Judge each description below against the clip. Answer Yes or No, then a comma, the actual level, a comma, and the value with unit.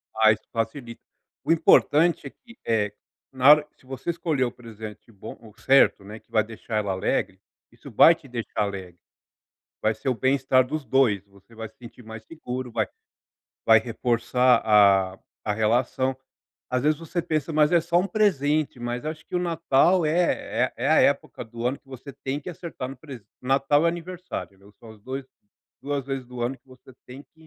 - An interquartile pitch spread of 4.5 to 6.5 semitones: Yes, average, 5.1 semitones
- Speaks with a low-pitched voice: Yes, low, 130 Hz